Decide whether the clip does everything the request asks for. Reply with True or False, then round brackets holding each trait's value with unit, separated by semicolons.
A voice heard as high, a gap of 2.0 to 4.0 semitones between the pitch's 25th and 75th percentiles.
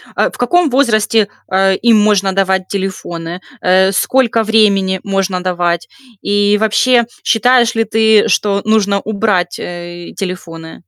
True (200 Hz; 3.0 semitones)